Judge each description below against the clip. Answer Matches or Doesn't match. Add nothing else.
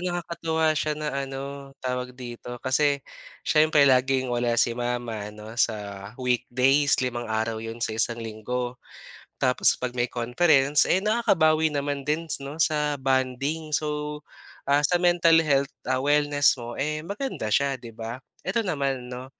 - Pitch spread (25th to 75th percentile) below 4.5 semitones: Matches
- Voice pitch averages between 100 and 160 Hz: Matches